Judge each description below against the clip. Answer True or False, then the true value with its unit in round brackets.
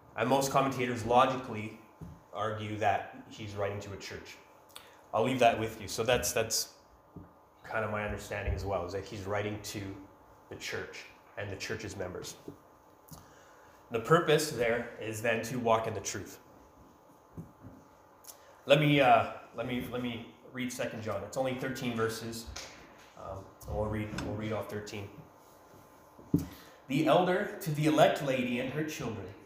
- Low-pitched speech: True (115 Hz)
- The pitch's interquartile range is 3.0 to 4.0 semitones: True (3.6 semitones)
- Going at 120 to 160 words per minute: True (155 wpm)